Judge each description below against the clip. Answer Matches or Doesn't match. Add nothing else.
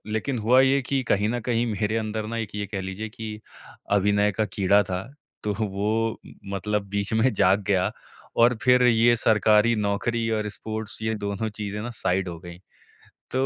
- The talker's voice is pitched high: Doesn't match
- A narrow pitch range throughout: Matches